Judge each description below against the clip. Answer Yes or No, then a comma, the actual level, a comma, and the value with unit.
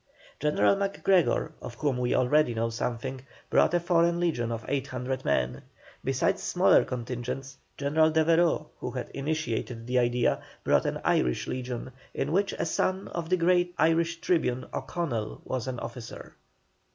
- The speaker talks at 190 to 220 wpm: No, average, 150 wpm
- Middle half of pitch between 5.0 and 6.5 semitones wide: Yes, wide, 5.4 semitones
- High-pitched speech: No, low, 135 Hz